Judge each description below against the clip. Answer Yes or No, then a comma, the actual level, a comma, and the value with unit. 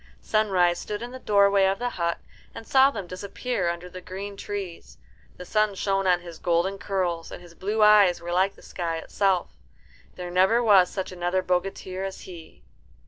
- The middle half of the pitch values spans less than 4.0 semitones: Yes, narrow, 2.4 semitones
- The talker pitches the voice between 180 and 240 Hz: Yes, high, 190 Hz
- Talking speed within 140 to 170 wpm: No, average, 185 wpm